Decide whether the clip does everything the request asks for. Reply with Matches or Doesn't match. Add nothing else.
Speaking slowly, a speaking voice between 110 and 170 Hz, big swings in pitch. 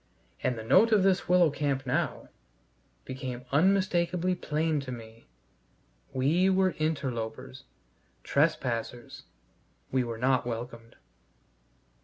Matches